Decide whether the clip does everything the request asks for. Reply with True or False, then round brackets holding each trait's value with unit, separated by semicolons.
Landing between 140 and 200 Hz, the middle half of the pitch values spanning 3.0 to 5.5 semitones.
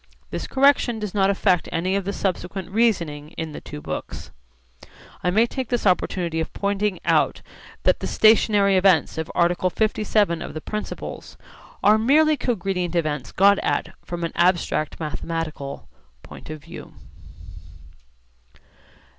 True (185 Hz; 4.2 semitones)